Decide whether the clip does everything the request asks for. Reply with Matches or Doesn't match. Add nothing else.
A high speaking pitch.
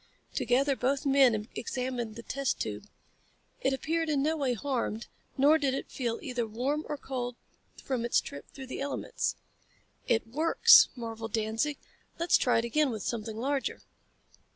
Matches